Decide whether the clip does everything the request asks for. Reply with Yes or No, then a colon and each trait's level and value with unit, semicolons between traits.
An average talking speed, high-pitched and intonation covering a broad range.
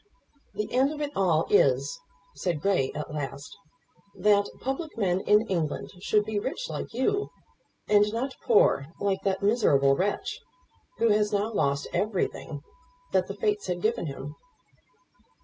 Yes: average, 150 wpm; high, 205 Hz; wide, 5.8 semitones